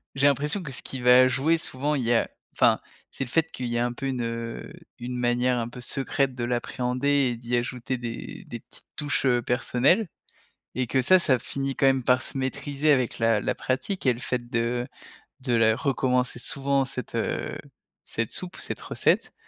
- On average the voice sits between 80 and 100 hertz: No, low, 130 Hz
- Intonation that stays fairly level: Yes, narrow, 2.2 semitones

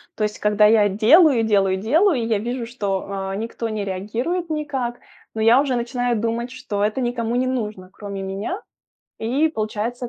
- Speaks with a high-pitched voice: Yes, high, 230 Hz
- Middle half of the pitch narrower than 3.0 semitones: No, average, 3.3 semitones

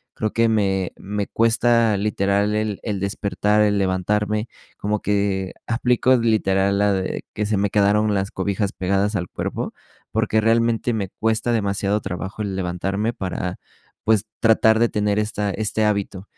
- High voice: No, low, 105 Hz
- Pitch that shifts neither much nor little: No, narrow, 1.8 semitones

